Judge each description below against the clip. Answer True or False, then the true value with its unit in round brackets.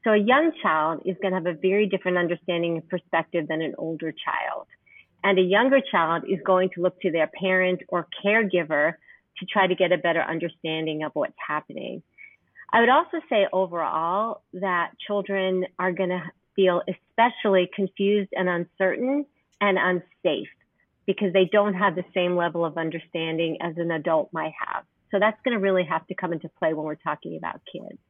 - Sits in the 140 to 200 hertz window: True (185 Hz)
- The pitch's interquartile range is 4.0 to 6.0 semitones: False (2.8 semitones)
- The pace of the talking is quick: False (185 wpm)